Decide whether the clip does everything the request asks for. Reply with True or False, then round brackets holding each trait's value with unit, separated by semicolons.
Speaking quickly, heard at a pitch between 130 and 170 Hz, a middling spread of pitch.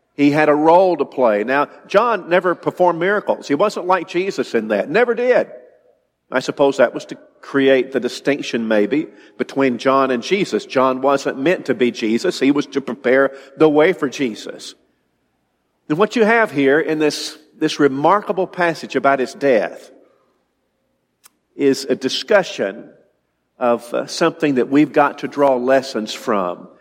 False (160 wpm; 140 Hz; 4.4 semitones)